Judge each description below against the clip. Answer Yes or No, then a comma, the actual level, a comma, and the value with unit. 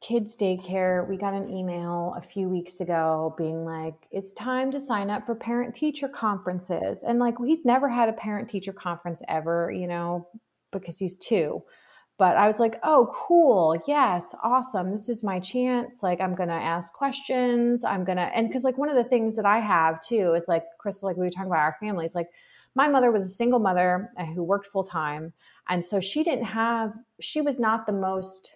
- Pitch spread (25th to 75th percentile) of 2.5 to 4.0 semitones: No, average, 5.1 semitones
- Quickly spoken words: Yes, fast, 210 wpm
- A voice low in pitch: No, high, 195 Hz